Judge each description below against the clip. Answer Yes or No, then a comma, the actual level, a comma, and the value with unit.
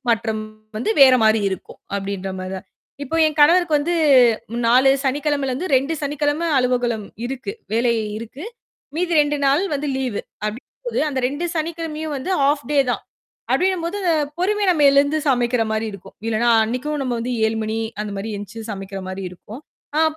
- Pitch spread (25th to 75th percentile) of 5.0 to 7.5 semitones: Yes, wide, 5.6 semitones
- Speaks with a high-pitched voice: Yes, very high, 260 Hz